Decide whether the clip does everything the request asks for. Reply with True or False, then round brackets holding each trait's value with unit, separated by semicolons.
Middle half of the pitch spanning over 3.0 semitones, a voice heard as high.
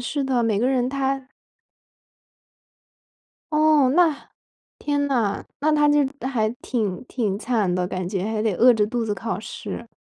True (4.5 semitones; 245 Hz)